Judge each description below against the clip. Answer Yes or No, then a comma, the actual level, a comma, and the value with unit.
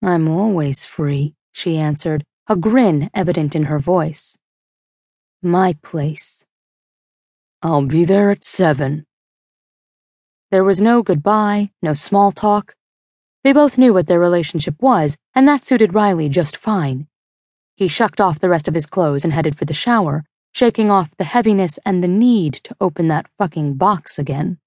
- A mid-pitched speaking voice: Yes, medium, 180 Hz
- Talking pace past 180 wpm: No, average, 155 wpm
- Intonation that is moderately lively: Yes, average, 4.9 semitones